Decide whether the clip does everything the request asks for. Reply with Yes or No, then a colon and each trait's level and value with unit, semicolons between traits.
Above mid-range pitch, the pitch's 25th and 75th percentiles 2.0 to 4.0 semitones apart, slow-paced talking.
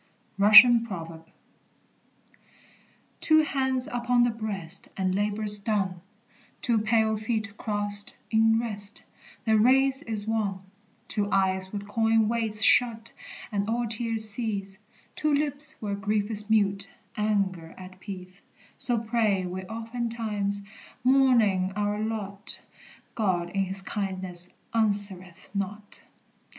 Yes: high, 210 Hz; narrow, 2.5 semitones; slow, 115 wpm